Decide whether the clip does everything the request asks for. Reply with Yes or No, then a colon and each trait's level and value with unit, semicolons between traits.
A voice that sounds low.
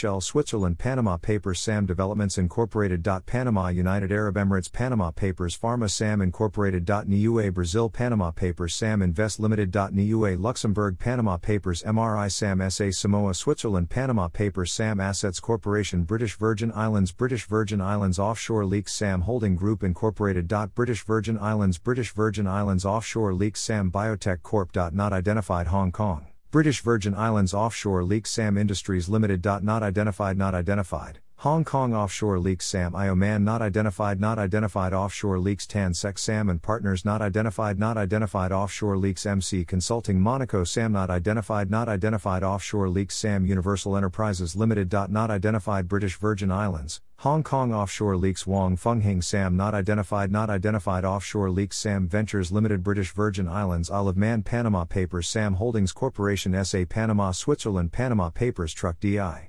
Yes: low, 100 Hz